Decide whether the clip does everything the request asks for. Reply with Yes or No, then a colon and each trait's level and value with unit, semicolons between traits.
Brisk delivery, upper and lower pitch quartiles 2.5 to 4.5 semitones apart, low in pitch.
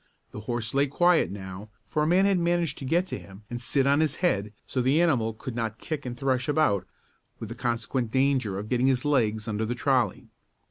No: fast, 220 wpm; average, 4.9 semitones; low, 130 Hz